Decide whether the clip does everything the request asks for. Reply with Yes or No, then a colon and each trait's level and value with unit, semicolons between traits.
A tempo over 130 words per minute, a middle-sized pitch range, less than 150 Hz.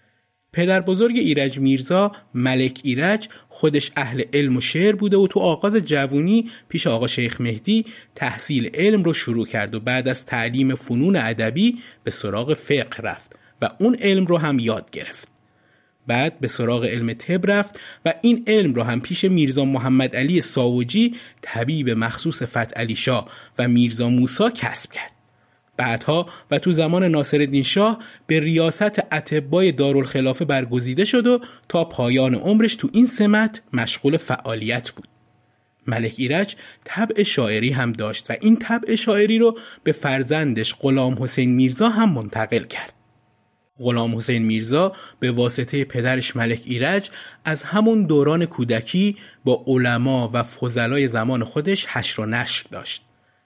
No: average, 150 wpm; wide, 7.5 semitones; medium, 140 Hz